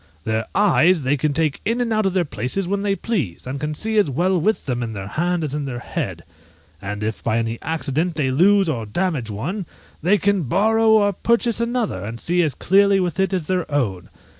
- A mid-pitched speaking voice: Yes, medium, 165 Hz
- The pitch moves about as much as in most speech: No, wide, 7.4 semitones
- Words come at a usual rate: No, fast, 220 wpm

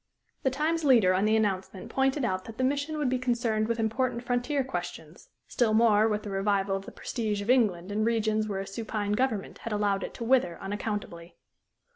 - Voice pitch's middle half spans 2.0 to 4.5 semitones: Yes, average, 3.7 semitones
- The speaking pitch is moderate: No, high, 220 Hz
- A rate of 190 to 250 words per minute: Yes, average, 200 wpm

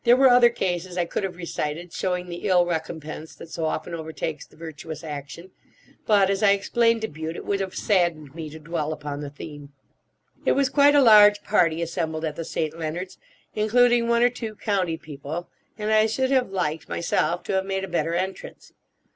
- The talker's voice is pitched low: No, medium, 175 Hz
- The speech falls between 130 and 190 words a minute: No, average, 200 wpm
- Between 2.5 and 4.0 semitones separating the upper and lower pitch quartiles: No, average, 4.9 semitones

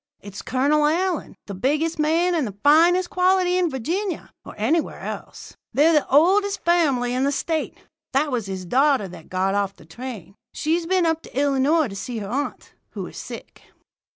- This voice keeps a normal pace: Yes, average, 180 wpm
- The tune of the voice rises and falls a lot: Yes, wide, 6.1 semitones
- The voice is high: Yes, very high, 290 Hz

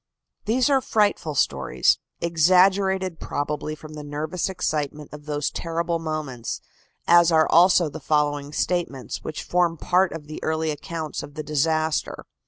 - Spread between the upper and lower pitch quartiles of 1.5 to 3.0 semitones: Yes, average, 2.7 semitones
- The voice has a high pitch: No, medium, 160 Hz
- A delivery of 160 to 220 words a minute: No, average, 145 wpm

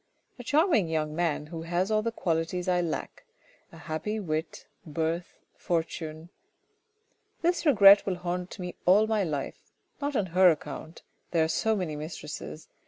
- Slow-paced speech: No, average, 165 wpm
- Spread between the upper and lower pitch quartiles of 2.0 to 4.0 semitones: No, average, 4.6 semitones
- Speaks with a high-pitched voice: No, medium, 175 Hz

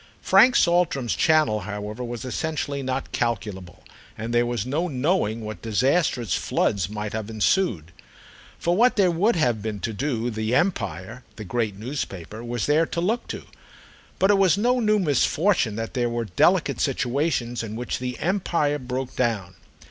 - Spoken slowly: No, average, 165 wpm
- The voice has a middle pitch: No, low, 125 Hz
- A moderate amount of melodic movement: No, wide, 6.9 semitones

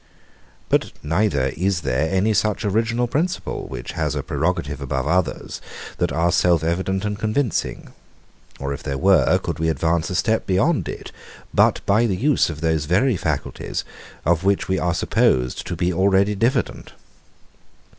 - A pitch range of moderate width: Yes, average, 4.5 semitones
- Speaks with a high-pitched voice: No, very low, 90 Hz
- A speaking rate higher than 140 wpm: Yes, average, 160 wpm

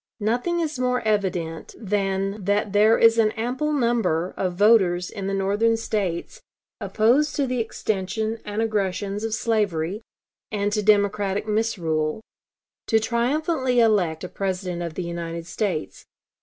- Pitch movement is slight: No, average, 3.3 semitones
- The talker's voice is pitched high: Yes, high, 210 Hz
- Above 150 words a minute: No, average, 140 wpm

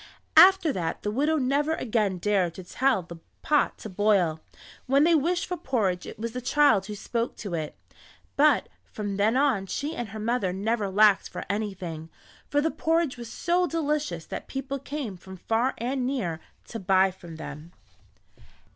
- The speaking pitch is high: Yes, high, 225 Hz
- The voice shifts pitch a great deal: Yes, wide, 6.8 semitones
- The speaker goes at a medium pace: Yes, average, 175 wpm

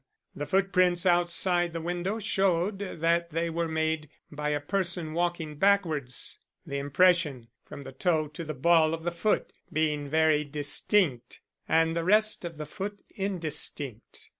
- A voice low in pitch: No, medium, 165 Hz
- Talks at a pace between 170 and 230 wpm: No, average, 150 wpm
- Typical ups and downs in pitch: Yes, average, 3.1 semitones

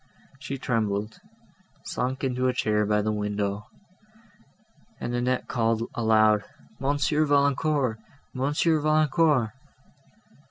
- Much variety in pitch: No, average, 4.7 semitones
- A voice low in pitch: Yes, low, 125 Hz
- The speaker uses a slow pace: Yes, slow, 95 wpm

